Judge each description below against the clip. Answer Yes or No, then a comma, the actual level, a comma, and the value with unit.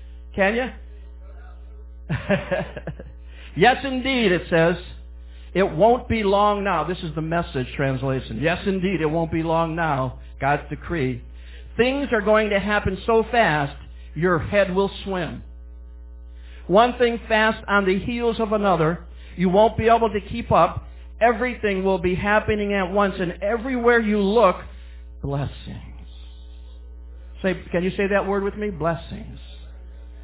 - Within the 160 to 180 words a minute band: No, average, 140 wpm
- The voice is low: No, medium, 170 Hz